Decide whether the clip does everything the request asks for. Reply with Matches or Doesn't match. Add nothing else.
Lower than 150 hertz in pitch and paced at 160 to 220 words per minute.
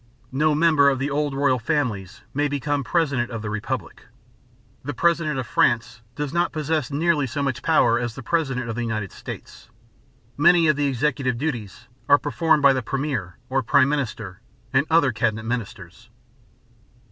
Matches